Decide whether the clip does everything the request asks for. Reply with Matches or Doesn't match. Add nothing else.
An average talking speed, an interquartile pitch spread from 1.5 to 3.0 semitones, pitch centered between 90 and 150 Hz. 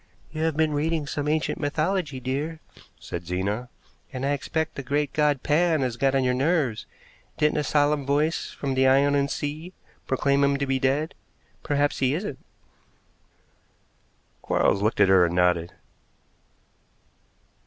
Matches